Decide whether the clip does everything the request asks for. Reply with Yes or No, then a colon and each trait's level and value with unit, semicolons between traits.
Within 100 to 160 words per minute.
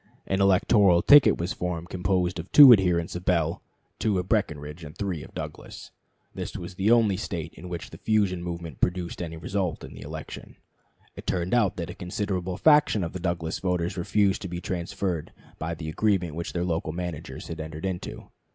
No: average, 190 wpm